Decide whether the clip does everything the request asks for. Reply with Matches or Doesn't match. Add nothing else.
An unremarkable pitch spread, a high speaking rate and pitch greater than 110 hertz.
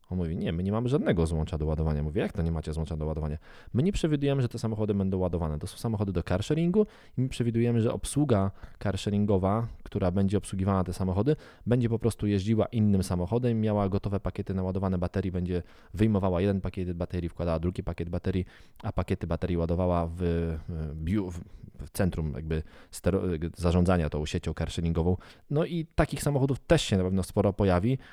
Doesn't match